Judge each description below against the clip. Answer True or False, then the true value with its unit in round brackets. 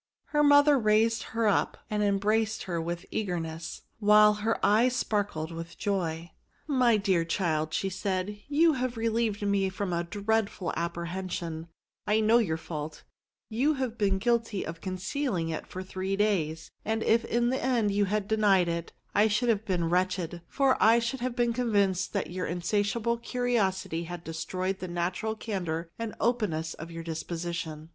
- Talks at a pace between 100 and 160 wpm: False (175 wpm)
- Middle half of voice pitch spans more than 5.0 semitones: False (4.6 semitones)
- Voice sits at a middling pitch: False (200 Hz)